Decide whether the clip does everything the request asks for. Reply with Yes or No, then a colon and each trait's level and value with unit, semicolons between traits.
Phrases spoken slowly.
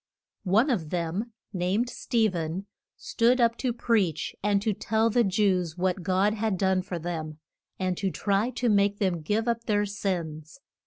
No: average, 170 wpm